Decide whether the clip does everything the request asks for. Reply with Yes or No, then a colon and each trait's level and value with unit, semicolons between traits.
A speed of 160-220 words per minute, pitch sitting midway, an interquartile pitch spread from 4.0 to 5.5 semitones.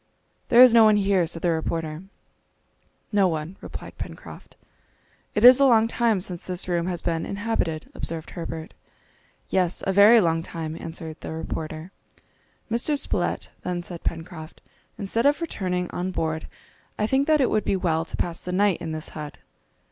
Yes: average, 170 wpm; medium, 180 Hz; average, 4.5 semitones